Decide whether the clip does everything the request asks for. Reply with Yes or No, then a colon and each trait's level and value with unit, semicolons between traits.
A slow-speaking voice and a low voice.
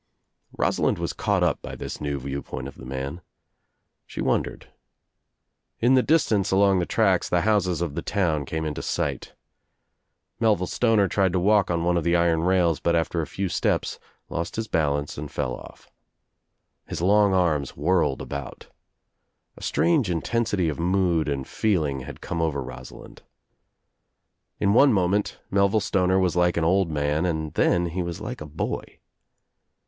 No: average, 170 wpm; very low, 85 Hz